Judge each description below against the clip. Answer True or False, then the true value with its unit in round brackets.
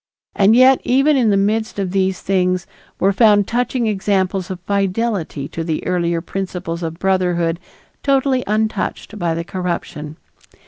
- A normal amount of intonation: True (3.7 semitones)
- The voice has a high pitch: True (195 Hz)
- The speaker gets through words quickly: False (145 wpm)